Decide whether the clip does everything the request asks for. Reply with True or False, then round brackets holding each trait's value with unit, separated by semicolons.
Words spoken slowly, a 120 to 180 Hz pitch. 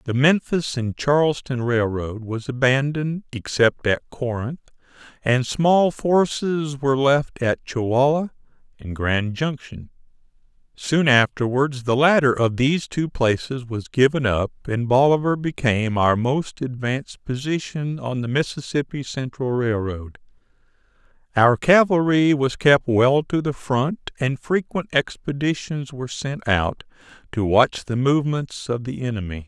True (130 wpm; 135 Hz)